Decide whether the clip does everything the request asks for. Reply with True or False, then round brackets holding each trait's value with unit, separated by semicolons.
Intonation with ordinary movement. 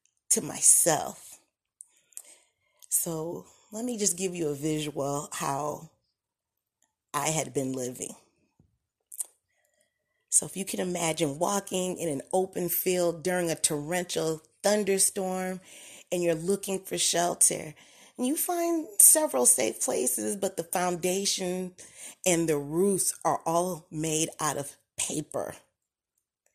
True (3.6 semitones)